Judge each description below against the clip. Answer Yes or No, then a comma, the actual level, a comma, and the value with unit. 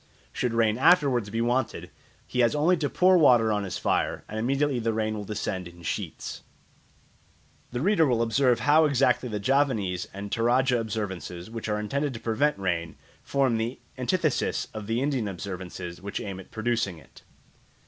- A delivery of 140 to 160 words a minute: No, average, 170 wpm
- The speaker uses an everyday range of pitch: Yes, average, 4.6 semitones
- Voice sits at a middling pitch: No, low, 115 Hz